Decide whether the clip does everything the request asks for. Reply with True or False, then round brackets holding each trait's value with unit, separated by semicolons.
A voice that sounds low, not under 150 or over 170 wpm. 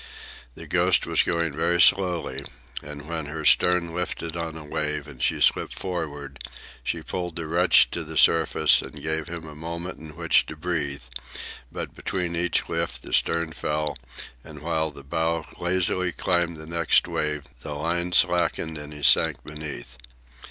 True (80 Hz; 165 wpm)